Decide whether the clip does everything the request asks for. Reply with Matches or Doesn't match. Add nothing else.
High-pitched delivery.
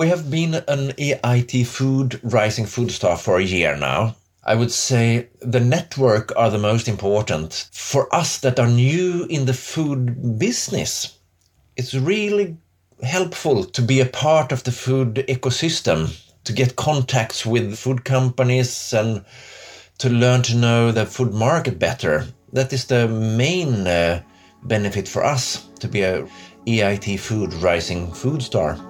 Doesn't match